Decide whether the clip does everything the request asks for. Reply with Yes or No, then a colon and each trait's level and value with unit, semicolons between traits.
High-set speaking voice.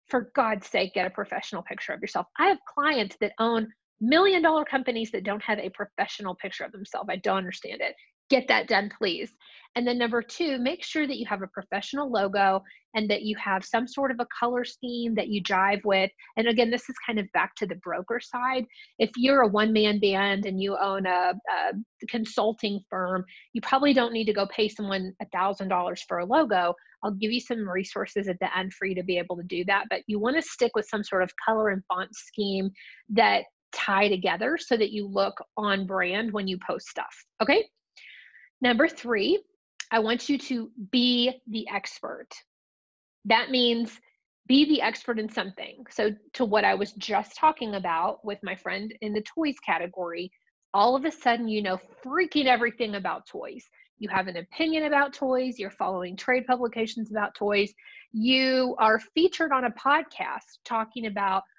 Yes: high, 220 Hz